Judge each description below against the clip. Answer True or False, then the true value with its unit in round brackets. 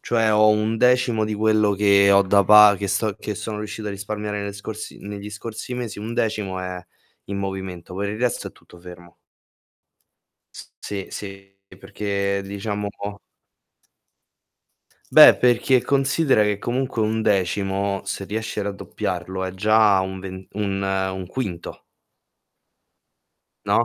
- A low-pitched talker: True (100 Hz)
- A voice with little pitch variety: True (1.9 semitones)